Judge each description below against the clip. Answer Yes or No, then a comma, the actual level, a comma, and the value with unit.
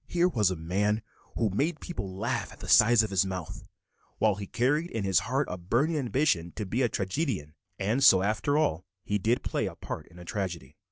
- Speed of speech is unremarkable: No, fast, 215 wpm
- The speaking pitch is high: No, low, 105 Hz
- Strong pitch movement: Yes, wide, 5.7 semitones